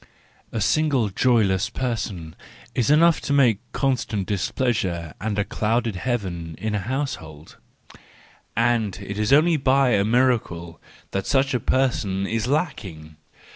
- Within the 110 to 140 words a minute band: Yes, slow, 135 wpm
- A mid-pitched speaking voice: No, low, 110 Hz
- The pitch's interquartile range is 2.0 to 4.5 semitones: No, average, 5.2 semitones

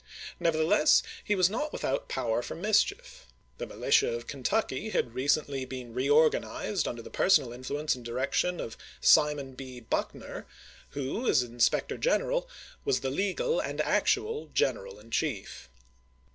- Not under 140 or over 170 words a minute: Yes, average, 145 wpm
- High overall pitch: No, medium, 150 Hz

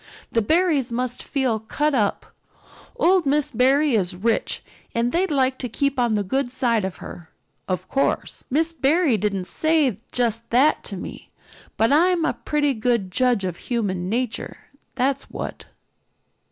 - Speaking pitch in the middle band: No, very high, 250 Hz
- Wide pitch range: No, average, 4.9 semitones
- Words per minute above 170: No, average, 155 wpm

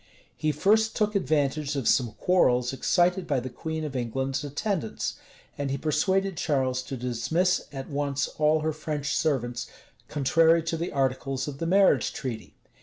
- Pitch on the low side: No, medium, 145 Hz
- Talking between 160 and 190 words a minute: Yes, average, 165 wpm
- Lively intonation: No, average, 3.8 semitones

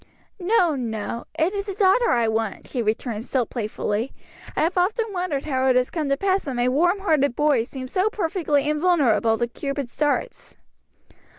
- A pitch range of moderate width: No, wide, 6.8 semitones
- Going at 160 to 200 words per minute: Yes, average, 180 wpm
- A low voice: No, very high, 285 Hz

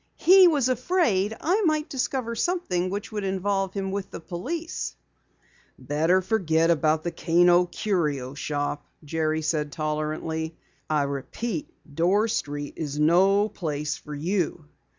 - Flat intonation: No, wide, 5.6 semitones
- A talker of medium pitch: Yes, medium, 175 Hz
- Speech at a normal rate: No, slow, 130 wpm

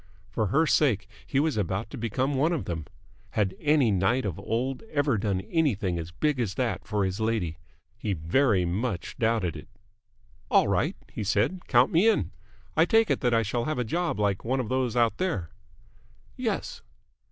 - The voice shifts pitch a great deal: Yes, wide, 5.7 semitones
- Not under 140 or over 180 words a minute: No, average, 190 wpm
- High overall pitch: No, low, 115 Hz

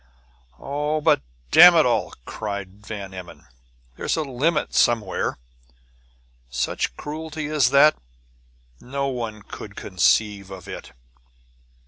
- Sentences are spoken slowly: Yes, slow, 110 wpm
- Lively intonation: Yes, wide, 7.1 semitones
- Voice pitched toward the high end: No, low, 120 Hz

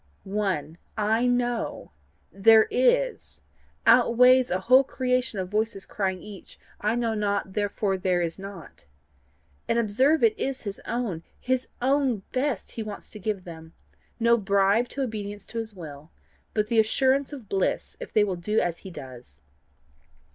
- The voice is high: Yes, high, 215 Hz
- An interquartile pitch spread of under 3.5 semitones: No, average, 4.3 semitones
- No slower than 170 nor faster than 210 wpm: No, average, 155 wpm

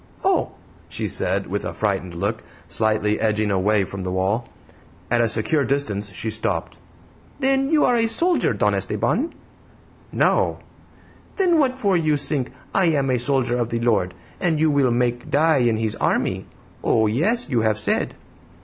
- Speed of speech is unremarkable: Yes, average, 165 wpm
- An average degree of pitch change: No, wide, 6.9 semitones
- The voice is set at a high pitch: No, low, 120 Hz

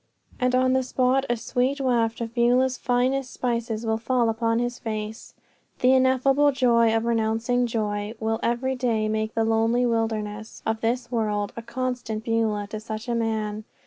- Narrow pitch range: Yes, narrow, 2.2 semitones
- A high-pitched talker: Yes, high, 230 Hz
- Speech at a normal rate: Yes, average, 170 wpm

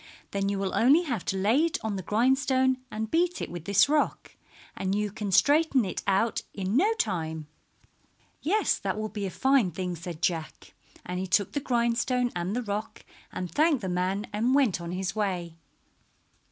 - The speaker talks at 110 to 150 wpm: No, average, 190 wpm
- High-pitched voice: Yes, high, 210 Hz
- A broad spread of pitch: Yes, wide, 5.8 semitones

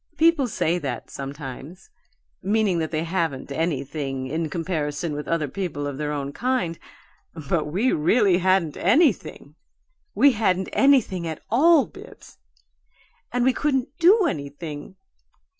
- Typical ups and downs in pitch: No, wide, 7.4 semitones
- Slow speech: Yes, slow, 130 wpm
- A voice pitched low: No, medium, 170 Hz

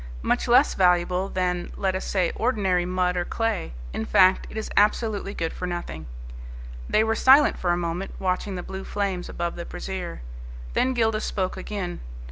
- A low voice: No, medium, 185 Hz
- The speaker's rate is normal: Yes, average, 175 wpm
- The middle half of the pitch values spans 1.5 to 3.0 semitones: Yes, average, 2.7 semitones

